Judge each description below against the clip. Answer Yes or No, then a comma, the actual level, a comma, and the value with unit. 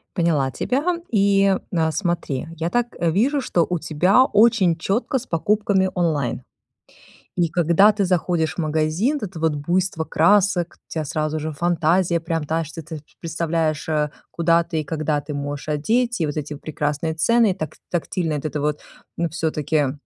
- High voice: No, medium, 165 Hz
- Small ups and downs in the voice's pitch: No, average, 3.5 semitones